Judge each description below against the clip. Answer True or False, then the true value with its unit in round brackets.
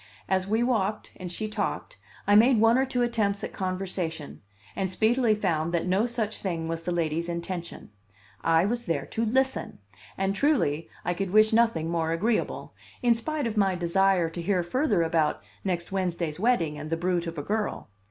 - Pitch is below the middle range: False (190 Hz)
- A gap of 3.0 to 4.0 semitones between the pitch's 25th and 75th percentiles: False (4.7 semitones)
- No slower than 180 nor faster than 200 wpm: True (185 wpm)